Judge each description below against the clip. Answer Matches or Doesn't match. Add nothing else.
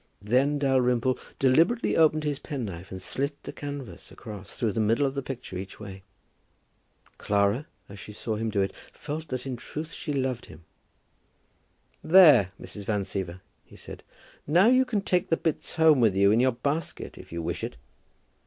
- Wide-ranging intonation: Matches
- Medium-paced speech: Matches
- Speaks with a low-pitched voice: Matches